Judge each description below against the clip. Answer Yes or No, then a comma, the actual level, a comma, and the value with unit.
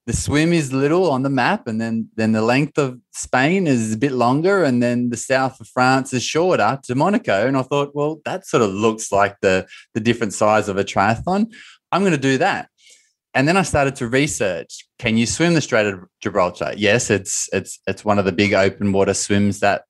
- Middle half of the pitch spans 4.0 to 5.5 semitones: Yes, average, 5.2 semitones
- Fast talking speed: Yes, fast, 225 wpm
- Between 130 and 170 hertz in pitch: No, low, 120 Hz